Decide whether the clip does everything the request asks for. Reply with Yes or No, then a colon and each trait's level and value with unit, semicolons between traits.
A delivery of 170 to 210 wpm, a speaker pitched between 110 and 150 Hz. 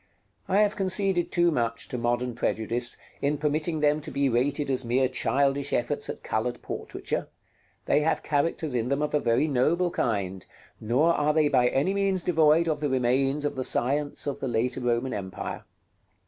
Yes: average, 180 wpm; medium, 140 Hz